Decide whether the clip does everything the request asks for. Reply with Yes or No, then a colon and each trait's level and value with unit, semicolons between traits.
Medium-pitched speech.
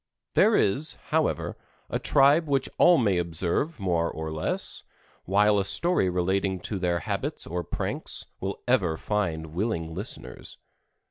No: very low, 95 Hz